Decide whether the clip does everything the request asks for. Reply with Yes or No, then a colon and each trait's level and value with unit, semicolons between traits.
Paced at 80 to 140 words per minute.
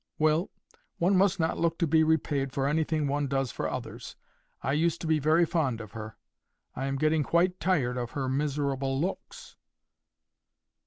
No: average, 170 wpm